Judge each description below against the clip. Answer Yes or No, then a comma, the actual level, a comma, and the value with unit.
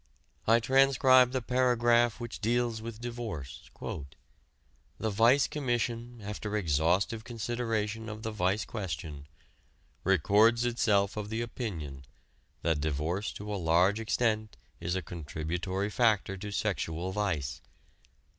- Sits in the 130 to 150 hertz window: No, low, 105 Hz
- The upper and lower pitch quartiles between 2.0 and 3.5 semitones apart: No, average, 4.4 semitones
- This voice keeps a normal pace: No, slow, 115 wpm